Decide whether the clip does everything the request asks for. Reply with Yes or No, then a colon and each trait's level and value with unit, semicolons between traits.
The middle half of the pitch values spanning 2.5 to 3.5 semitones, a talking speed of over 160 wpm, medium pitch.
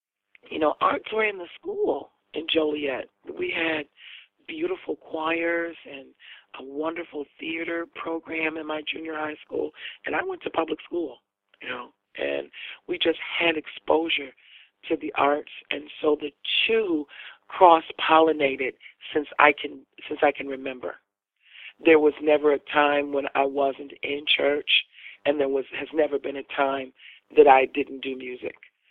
No: average, 2.8 semitones; average, 155 wpm; medium, 150 Hz